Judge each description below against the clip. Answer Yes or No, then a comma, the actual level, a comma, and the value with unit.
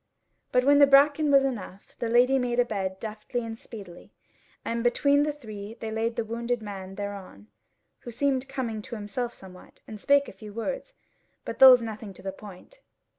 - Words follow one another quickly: No, average, 185 wpm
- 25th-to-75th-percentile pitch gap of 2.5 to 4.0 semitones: No, average, 4.4 semitones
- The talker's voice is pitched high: Yes, high, 230 Hz